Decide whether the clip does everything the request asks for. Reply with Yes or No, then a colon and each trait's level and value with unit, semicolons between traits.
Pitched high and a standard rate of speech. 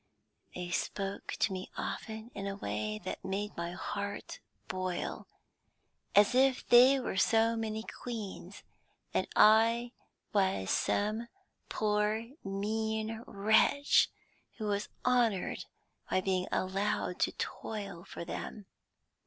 No: high, 210 Hz; slow, 115 wpm